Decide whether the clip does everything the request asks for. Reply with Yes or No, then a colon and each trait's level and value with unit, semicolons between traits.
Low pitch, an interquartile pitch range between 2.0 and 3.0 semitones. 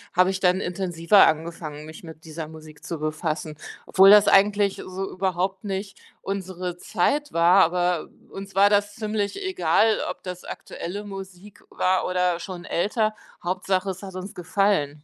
No: medium, 185 Hz; narrow, 2.5 semitones